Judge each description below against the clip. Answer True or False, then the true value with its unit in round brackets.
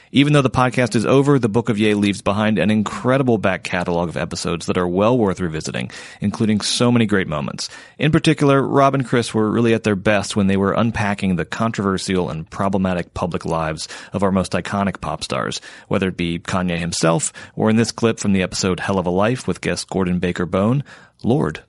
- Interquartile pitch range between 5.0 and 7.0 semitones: False (4.2 semitones)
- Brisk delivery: True (210 wpm)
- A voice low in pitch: True (100 Hz)